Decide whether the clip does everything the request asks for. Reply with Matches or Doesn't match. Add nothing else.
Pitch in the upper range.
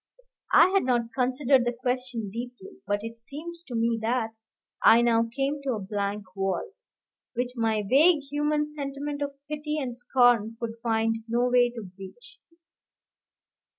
Matches